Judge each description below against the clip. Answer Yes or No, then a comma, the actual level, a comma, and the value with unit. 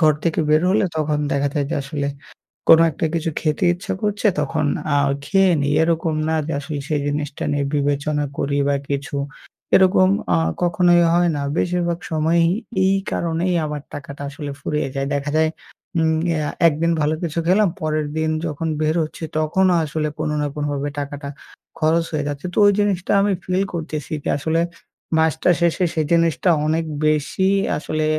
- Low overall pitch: No, medium, 155 Hz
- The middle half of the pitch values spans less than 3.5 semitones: Yes, narrow, 2.6 semitones